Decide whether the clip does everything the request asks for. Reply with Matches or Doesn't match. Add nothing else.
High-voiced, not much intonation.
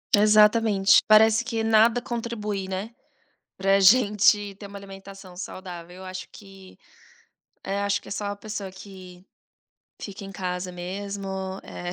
Matches